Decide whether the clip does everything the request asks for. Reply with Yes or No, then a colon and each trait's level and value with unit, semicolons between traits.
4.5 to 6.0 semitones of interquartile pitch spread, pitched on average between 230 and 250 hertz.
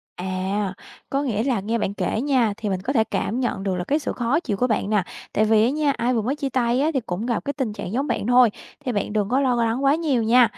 No: average, 4.0 semitones; high, 235 Hz